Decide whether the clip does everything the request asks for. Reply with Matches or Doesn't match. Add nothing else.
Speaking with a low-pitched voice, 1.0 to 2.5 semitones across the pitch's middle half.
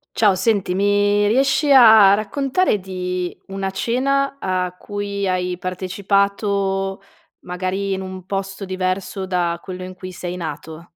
Doesn't match